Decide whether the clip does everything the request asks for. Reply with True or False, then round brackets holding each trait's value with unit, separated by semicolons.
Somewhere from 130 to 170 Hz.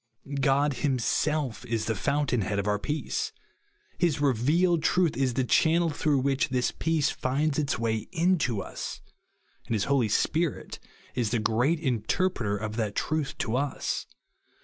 True (135 Hz)